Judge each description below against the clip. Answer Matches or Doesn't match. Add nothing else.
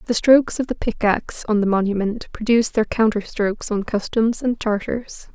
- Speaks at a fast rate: Doesn't match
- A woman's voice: Matches